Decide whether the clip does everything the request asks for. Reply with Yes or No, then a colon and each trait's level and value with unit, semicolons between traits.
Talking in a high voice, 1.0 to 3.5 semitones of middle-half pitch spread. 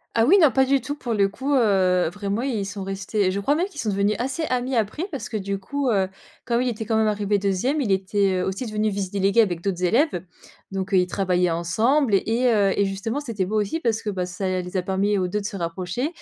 No: high, 205 Hz; average, 4.1 semitones